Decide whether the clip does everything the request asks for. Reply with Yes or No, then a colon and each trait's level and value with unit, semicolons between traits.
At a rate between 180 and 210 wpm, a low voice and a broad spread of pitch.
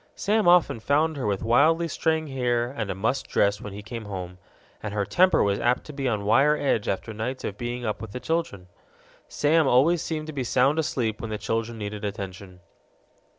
Yes: fast, 205 wpm; low, 120 Hz; wide, 6.0 semitones